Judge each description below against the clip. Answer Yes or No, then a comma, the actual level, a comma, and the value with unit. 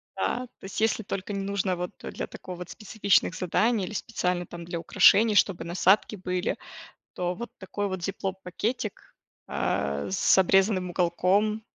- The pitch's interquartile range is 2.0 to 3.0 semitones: Yes, narrow, 2.5 semitones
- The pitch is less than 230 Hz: Yes, high, 190 Hz